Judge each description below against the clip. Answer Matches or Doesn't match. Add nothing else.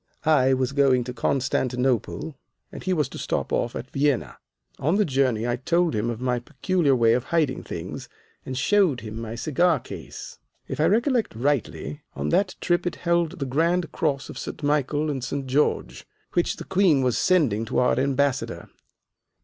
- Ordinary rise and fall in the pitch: Matches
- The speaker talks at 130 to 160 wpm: Doesn't match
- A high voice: Doesn't match